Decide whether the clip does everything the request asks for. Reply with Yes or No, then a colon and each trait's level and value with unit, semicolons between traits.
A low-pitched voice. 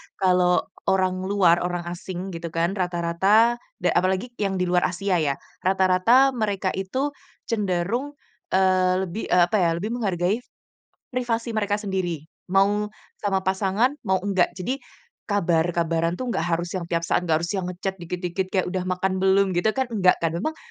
No: medium, 185 Hz